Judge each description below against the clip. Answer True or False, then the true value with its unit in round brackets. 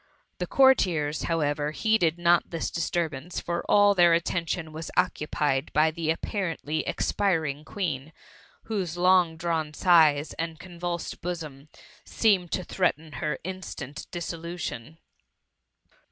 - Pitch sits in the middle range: True (165 Hz)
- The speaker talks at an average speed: False (120 wpm)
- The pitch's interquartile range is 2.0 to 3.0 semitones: True (2.5 semitones)